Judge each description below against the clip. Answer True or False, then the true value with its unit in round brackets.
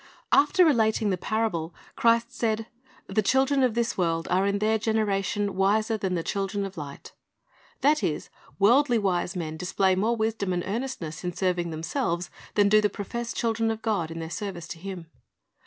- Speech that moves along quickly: False (180 wpm)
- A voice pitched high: True (200 Hz)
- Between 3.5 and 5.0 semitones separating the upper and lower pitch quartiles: True (3.9 semitones)